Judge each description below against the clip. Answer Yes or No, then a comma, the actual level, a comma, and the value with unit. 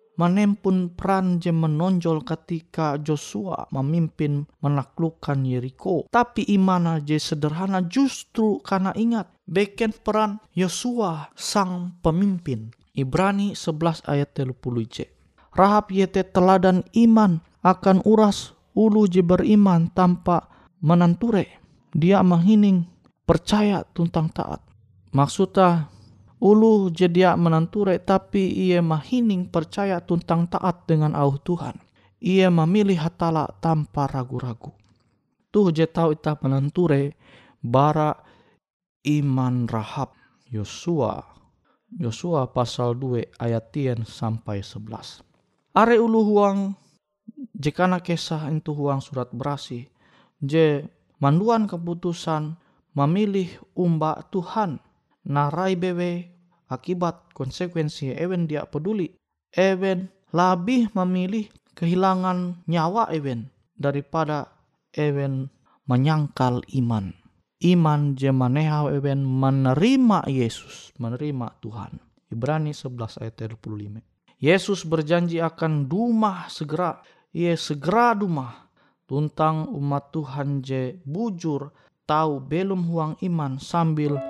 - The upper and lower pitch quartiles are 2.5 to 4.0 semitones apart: No, average, 5.0 semitones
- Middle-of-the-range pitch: Yes, medium, 165 Hz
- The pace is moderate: Yes, average, 95 wpm